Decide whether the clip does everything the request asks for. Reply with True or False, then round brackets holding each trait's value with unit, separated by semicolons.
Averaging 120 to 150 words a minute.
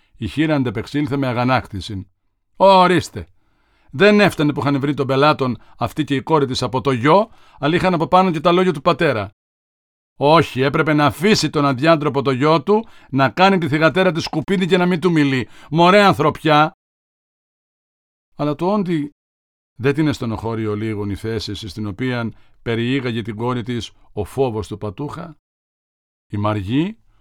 False (165 wpm)